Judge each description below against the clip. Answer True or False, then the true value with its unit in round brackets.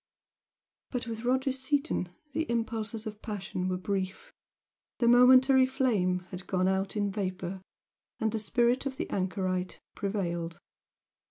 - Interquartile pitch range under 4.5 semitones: False (5.2 semitones)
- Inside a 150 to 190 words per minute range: False (135 wpm)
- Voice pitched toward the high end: True (215 Hz)